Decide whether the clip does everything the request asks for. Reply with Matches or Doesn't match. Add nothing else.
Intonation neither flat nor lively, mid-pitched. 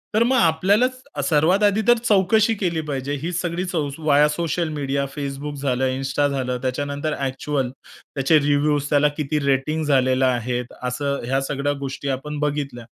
Matches